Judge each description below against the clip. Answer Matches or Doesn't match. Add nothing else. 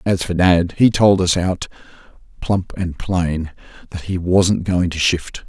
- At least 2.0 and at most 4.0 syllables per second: Matches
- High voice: Doesn't match